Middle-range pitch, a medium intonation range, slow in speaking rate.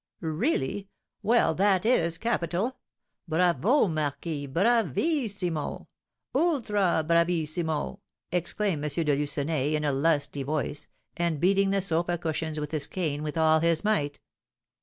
Yes: medium, 165 Hz; average, 4.5 semitones; slow, 120 wpm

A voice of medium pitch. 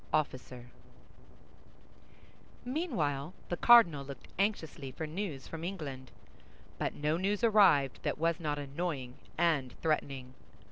Yes: medium, 155 Hz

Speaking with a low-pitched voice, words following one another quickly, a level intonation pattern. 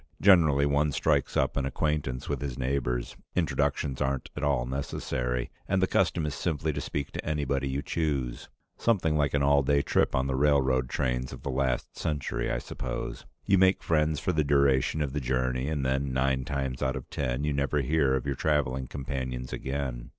No: very low, 70 Hz; average, 195 wpm; narrow, 2.3 semitones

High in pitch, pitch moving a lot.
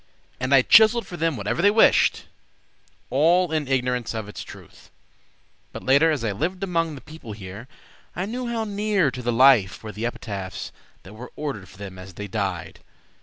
No: low, 130 Hz; wide, 8.3 semitones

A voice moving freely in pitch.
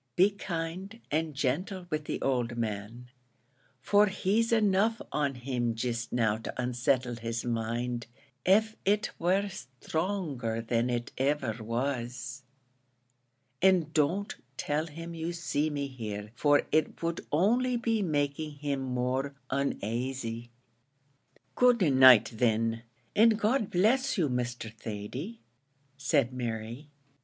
Yes: wide, 7.2 semitones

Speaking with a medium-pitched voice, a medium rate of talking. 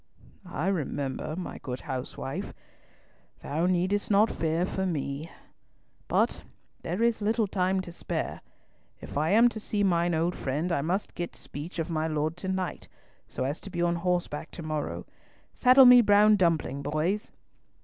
Yes: medium, 175 Hz; average, 160 wpm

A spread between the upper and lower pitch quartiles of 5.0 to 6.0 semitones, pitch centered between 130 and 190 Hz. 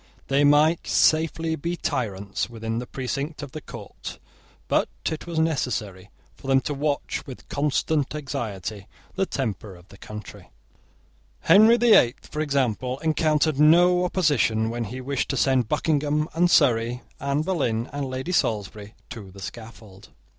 Yes: wide, 5.4 semitones; low, 135 Hz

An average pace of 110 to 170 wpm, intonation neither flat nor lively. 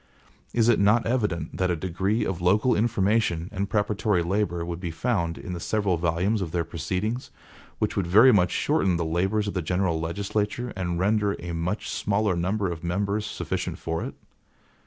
No: average, 180 wpm; average, 3.5 semitones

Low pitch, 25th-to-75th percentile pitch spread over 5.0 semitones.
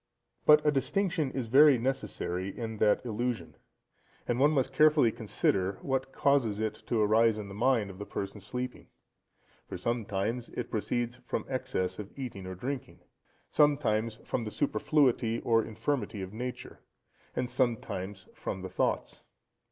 No: low, 115 Hz; average, 4.0 semitones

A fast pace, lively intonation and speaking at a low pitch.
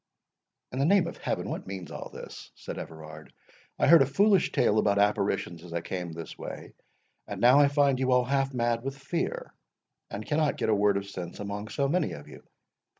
Yes: fast, 210 wpm; wide, 6.2 semitones; low, 120 Hz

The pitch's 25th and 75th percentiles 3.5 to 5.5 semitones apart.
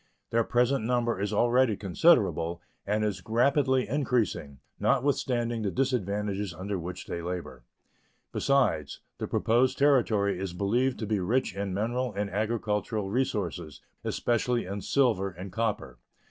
Yes: average, 4.3 semitones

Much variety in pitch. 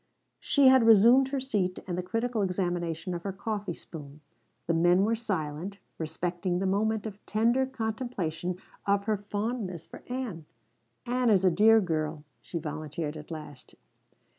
No: average, 4.9 semitones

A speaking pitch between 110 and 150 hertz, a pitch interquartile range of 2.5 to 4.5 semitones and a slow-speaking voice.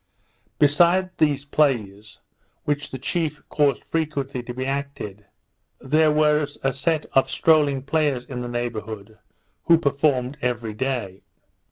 Yes: medium, 140 Hz; average, 3.6 semitones; slow, 125 wpm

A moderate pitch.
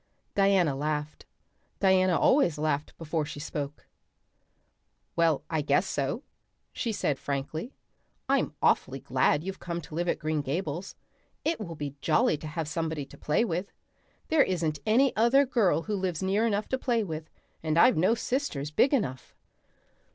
Yes: medium, 170 Hz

